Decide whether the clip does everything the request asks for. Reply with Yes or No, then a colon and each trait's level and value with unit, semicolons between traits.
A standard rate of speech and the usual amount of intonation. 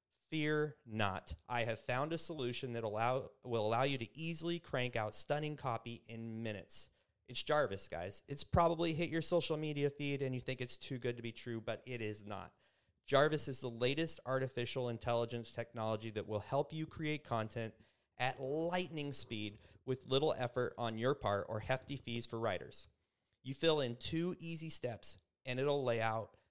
Yes: average, 180 wpm; average, 4.3 semitones